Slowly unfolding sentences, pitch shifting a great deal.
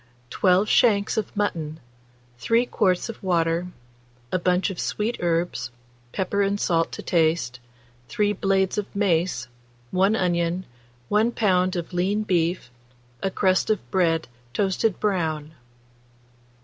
No: slow, 125 wpm; average, 3.3 semitones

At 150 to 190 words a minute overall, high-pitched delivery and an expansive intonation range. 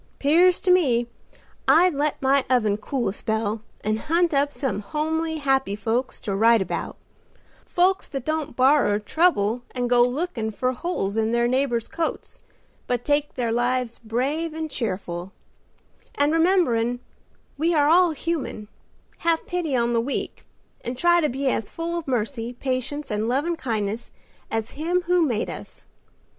Yes: average, 155 wpm; very high, 260 Hz; wide, 5.7 semitones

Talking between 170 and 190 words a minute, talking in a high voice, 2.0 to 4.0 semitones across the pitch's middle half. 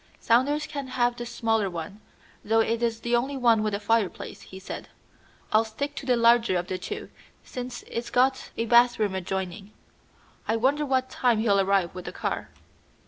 Yes: average, 185 wpm; high, 230 Hz; average, 3.5 semitones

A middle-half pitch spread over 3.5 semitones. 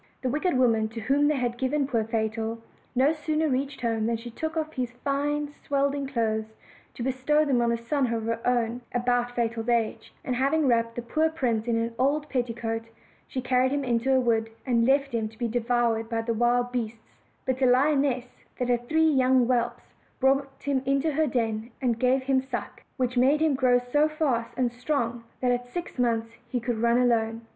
No: average, 2.9 semitones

